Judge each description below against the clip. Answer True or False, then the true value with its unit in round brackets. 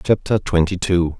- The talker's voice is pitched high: False (90 Hz)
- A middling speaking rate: True (150 wpm)